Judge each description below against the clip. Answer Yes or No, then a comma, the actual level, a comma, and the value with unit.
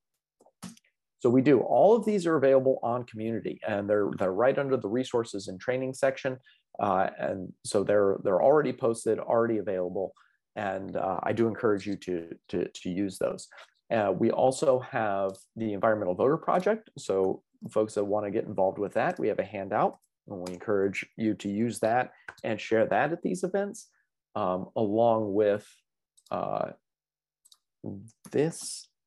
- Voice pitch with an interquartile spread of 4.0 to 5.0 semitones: Yes, average, 4.3 semitones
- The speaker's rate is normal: Yes, average, 165 wpm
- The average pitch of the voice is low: Yes, low, 110 Hz